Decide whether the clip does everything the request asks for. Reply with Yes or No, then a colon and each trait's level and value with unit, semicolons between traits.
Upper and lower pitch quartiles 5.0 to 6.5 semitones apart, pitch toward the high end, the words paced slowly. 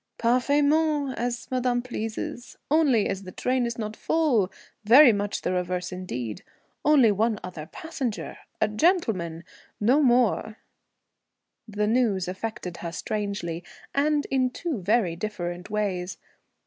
Yes: wide, 5.4 semitones; high, 220 Hz; slow, 130 wpm